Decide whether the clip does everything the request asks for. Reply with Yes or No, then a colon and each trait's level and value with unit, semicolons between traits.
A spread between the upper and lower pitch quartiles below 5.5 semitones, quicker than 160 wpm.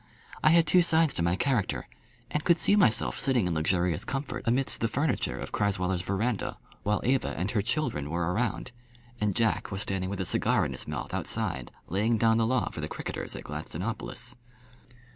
No: wide, 5.9 semitones; average, 190 wpm